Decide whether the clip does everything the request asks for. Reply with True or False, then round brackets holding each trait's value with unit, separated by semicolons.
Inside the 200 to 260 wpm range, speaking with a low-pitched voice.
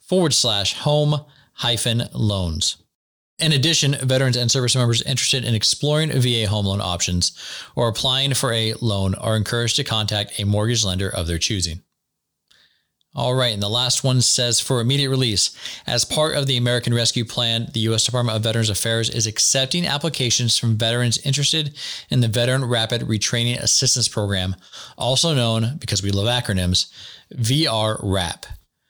False (160 wpm; 120 Hz)